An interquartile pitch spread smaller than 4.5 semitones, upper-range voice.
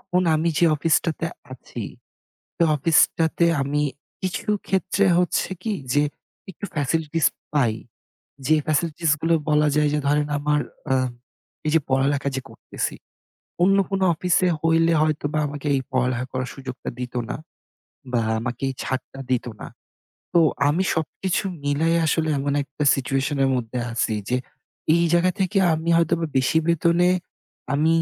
No: average, 3.7 semitones; medium, 150 Hz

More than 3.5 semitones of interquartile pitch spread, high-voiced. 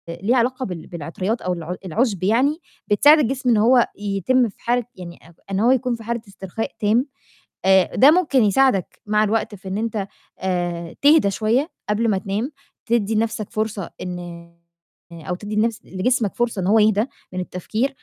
Yes: average, 4.1 semitones; high, 215 Hz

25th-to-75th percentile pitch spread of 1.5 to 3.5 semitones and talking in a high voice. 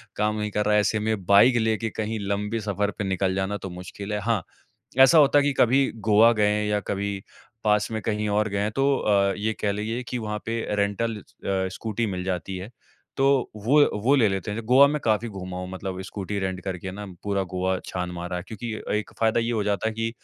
No: narrow, 2.5 semitones; low, 105 Hz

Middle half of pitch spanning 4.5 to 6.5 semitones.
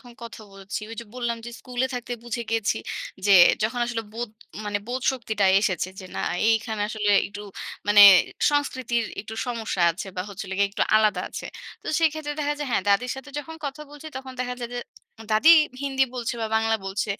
No: average, 3.7 semitones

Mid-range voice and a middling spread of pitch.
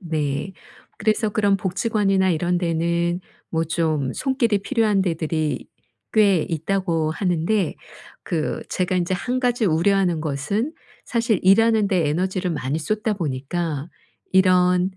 Yes: medium, 180 Hz; average, 4.0 semitones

